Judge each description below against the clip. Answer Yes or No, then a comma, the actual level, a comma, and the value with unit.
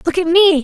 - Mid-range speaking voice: No, very high, 345 Hz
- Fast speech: Yes, fast, 285 wpm